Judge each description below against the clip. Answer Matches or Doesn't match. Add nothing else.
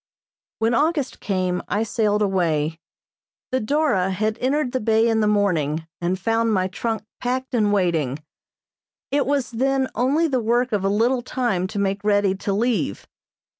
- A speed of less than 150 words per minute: Doesn't match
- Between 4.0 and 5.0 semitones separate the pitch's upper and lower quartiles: Matches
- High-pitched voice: Matches